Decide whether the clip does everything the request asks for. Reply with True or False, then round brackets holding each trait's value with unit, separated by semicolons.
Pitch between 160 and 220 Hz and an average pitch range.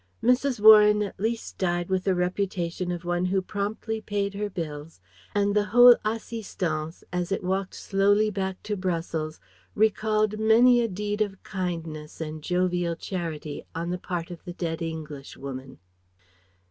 True (185 Hz; 3.7 semitones)